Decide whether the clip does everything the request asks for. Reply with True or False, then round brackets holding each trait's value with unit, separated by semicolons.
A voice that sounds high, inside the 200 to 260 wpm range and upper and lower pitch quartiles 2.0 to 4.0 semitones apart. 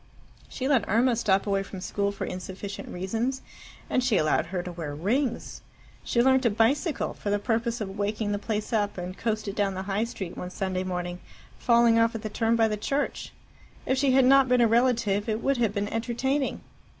True (220 Hz; 205 wpm; 3.5 semitones)